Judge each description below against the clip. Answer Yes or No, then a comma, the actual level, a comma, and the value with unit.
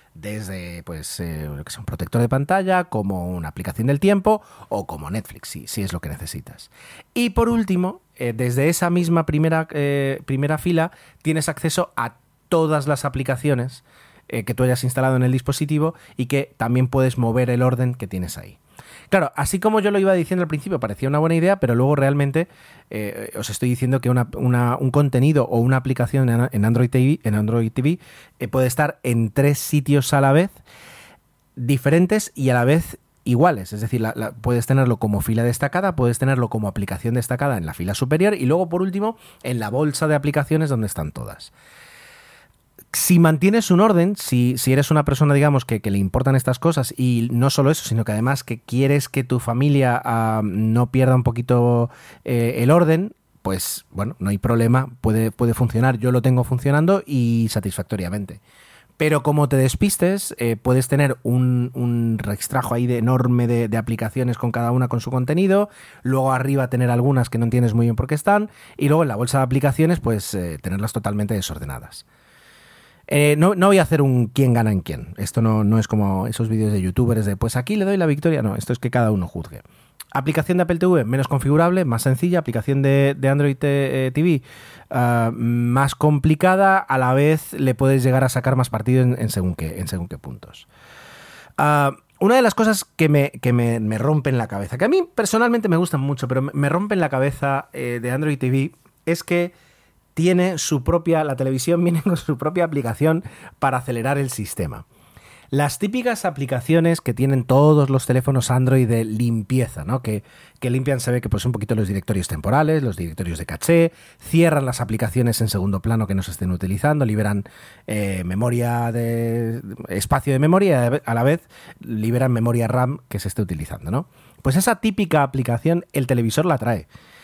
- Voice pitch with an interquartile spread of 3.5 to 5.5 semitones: Yes, average, 4.6 semitones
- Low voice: Yes, low, 130 Hz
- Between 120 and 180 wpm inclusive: No, fast, 190 wpm